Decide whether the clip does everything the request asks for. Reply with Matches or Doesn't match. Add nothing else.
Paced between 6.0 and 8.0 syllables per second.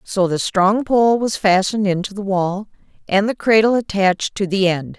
Doesn't match